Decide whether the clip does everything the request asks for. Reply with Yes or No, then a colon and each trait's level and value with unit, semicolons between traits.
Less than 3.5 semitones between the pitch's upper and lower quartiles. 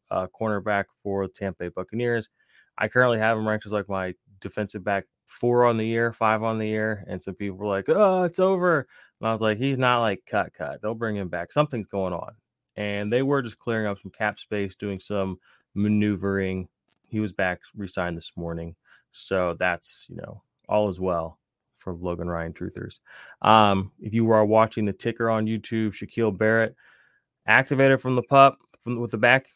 Yes: average, 2.9 semitones